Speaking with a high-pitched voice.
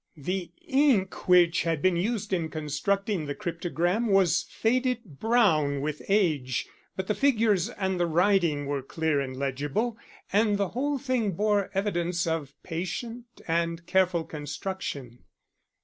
No: medium, 180 Hz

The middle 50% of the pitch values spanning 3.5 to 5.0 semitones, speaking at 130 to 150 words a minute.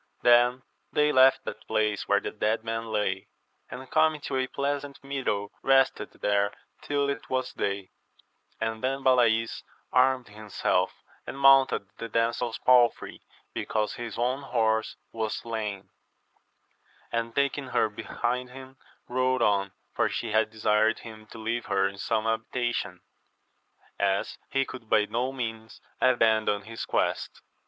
No: average, 3.0 semitones; average, 145 wpm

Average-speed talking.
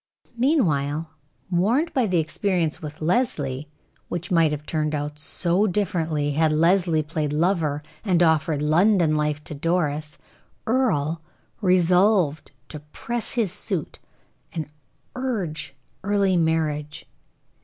No: slow, 115 wpm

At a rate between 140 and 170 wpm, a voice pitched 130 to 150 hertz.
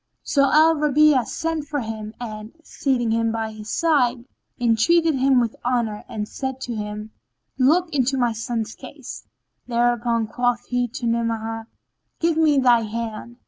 No: average, 150 wpm; high, 240 Hz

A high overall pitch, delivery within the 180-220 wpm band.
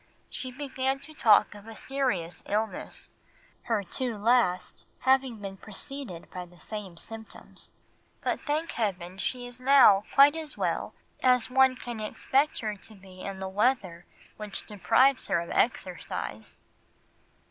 No: high, 220 Hz; average, 145 wpm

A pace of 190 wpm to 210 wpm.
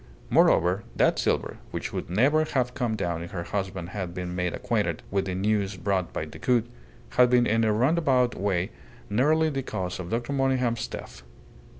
No: average, 180 wpm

